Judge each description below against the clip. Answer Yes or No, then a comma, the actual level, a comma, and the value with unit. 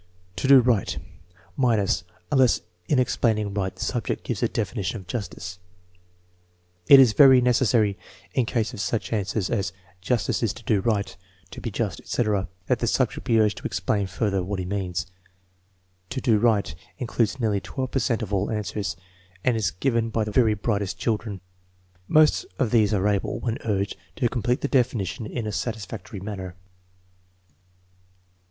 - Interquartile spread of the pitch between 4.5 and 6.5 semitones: No, average, 3.2 semitones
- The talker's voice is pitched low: Yes, low, 110 Hz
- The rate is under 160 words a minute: No, average, 165 wpm